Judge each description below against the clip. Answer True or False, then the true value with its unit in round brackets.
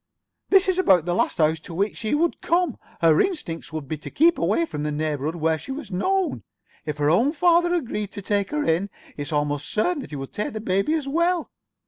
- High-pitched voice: True (205 Hz)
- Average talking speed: False (225 wpm)